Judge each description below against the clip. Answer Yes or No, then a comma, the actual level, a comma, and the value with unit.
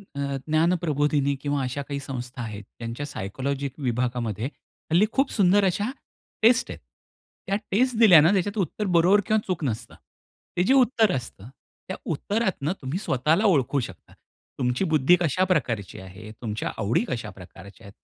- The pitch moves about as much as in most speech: No, wide, 7.3 semitones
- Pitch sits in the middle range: Yes, medium, 145 Hz